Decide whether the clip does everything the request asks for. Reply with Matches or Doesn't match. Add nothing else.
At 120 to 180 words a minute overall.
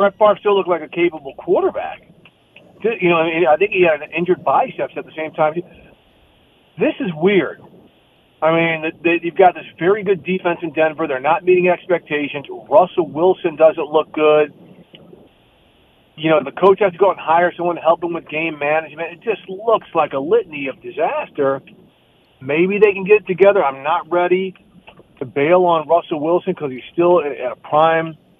Doesn't match